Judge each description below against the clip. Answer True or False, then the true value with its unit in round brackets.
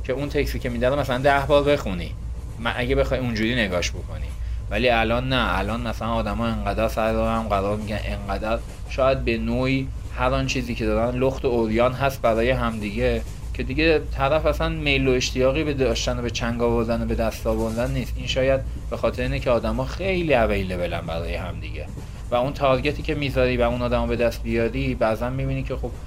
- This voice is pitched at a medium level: False (120 Hz)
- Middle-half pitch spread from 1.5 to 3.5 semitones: True (3.2 semitones)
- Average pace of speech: False (195 wpm)